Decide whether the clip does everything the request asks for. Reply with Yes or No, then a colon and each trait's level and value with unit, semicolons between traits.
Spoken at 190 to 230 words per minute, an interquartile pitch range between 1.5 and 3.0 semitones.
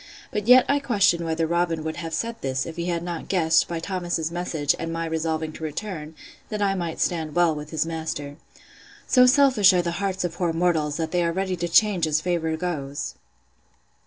Yes: fast, 205 wpm; narrow, 2.4 semitones